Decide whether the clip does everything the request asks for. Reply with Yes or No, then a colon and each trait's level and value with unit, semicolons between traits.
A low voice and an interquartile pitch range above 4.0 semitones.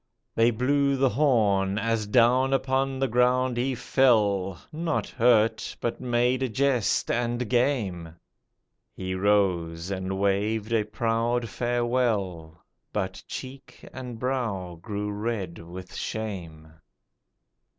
Yes: low, 115 Hz; average, 4.4 semitones